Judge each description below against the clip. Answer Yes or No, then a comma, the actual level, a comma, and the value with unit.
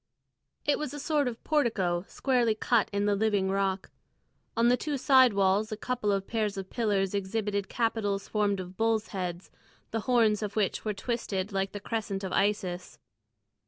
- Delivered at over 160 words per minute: Yes, average, 175 wpm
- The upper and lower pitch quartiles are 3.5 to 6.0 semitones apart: No, average, 2.9 semitones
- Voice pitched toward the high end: Yes, high, 210 Hz